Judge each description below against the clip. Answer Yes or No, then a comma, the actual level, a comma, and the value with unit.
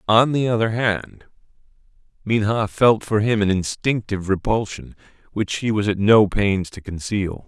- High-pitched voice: No, low, 105 Hz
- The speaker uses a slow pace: No, average, 155 wpm